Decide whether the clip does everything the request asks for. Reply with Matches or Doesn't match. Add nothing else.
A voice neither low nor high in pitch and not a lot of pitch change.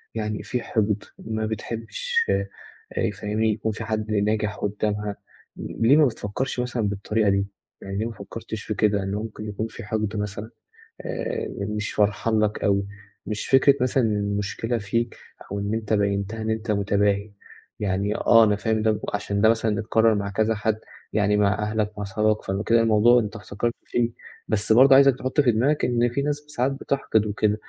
Doesn't match